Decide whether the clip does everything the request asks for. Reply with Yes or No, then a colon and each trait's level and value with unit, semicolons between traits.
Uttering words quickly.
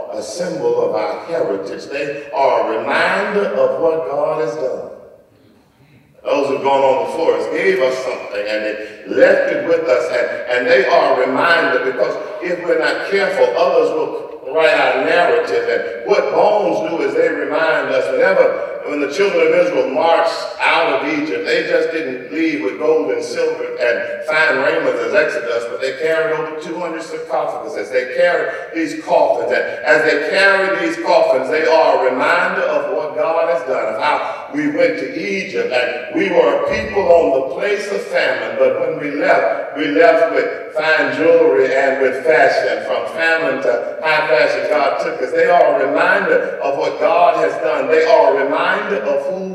No: average, 185 wpm